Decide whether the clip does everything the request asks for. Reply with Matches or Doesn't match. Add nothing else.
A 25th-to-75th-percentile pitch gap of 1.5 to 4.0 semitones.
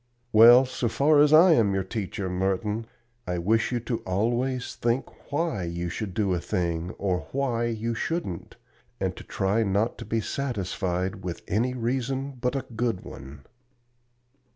Doesn't match